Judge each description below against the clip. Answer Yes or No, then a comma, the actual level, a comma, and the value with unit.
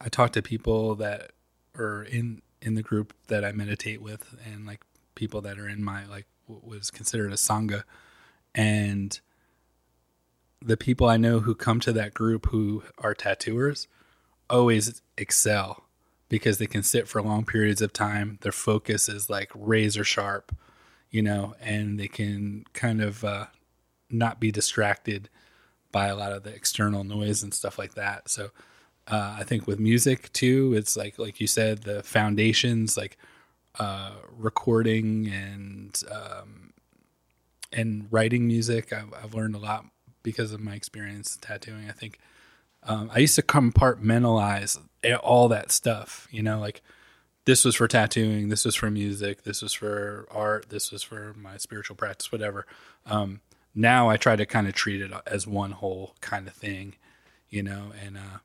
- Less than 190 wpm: Yes, average, 165 wpm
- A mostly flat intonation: Yes, narrow, 1.8 semitones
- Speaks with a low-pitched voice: Yes, low, 105 Hz